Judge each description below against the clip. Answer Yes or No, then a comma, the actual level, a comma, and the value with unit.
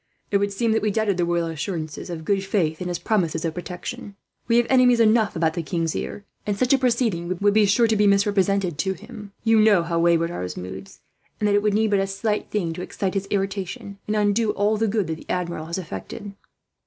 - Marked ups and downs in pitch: No, average, 3.7 semitones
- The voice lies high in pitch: Yes, high, 200 Hz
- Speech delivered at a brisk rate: Yes, fast, 230 wpm